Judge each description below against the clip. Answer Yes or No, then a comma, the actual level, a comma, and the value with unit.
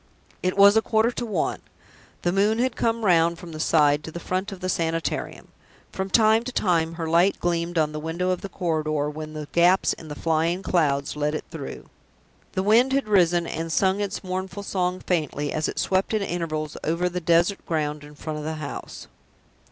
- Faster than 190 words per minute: Yes, fast, 205 wpm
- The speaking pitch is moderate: Yes, medium, 170 Hz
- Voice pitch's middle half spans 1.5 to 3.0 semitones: No, average, 3.6 semitones